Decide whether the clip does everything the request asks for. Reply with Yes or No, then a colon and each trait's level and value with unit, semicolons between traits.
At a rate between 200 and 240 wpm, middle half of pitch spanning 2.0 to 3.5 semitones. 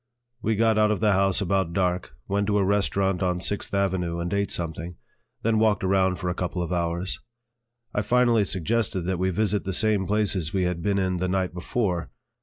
Yes: fast, 205 wpm; narrow, 2.4 semitones